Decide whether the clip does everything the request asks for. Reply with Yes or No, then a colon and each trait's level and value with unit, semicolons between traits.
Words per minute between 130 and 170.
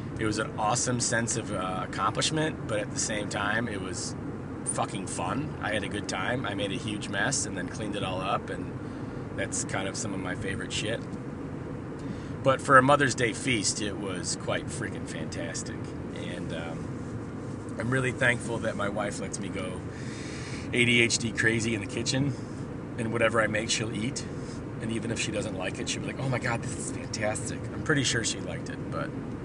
No: average, 200 wpm